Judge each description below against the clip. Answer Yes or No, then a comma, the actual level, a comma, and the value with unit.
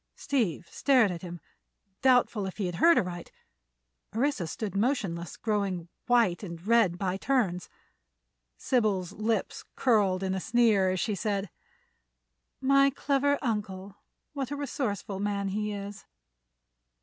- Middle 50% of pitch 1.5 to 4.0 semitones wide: No, average, 4.6 semitones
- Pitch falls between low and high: No, high, 205 Hz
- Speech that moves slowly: Yes, slow, 125 wpm